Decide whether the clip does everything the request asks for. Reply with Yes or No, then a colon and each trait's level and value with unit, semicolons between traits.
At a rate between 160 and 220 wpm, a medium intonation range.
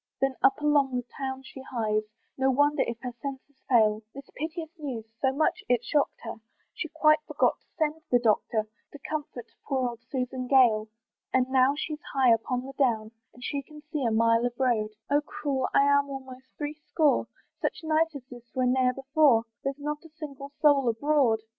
Yes: average, 190 wpm; average, 3.2 semitones